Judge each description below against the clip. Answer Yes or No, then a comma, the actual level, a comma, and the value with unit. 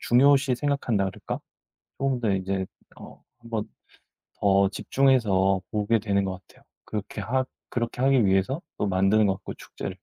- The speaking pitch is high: No, low, 105 Hz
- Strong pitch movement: No, average, 4.6 semitones